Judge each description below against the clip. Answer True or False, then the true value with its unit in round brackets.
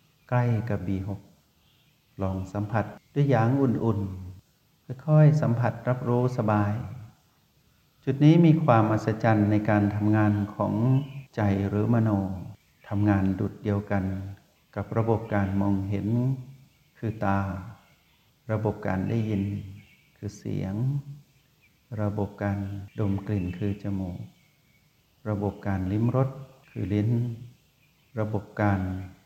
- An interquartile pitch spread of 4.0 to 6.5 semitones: False (3.3 semitones)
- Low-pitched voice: True (105 Hz)